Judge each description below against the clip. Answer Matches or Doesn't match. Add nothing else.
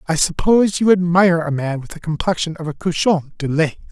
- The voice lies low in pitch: Doesn't match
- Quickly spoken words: Matches